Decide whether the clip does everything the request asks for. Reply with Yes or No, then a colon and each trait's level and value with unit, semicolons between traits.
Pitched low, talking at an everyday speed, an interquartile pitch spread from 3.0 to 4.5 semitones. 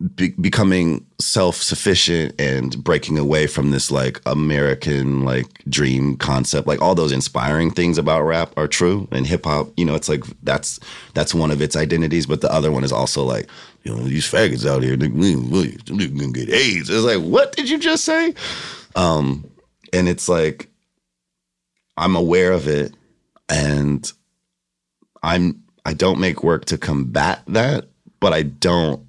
Yes: very low, 75 Hz; average, 160 wpm; average, 4.0 semitones